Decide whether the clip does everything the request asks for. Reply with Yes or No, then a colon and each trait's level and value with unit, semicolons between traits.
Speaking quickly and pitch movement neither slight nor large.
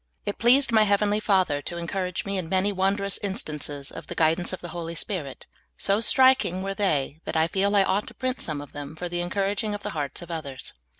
Yes: fast, 225 wpm; average, 4.0 semitones